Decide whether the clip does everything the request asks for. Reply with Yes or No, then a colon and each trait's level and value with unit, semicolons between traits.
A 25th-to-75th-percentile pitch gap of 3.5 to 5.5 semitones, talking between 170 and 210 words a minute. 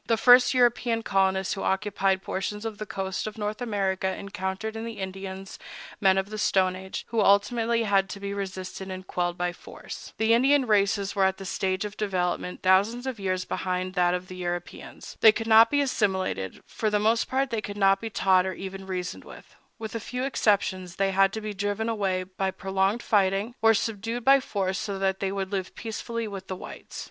No: average, 2.7 semitones; fast, 205 wpm